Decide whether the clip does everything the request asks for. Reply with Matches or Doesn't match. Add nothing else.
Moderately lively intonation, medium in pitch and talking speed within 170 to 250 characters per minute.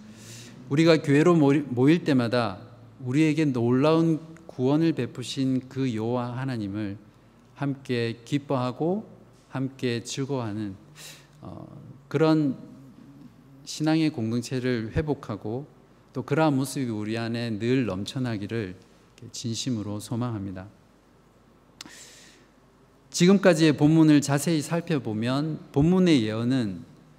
Doesn't match